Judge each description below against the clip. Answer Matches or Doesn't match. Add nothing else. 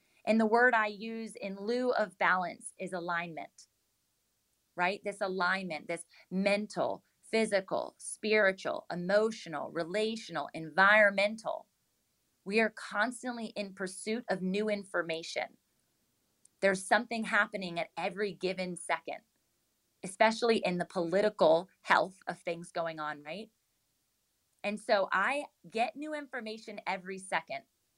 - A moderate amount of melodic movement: Matches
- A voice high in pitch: Matches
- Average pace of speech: Doesn't match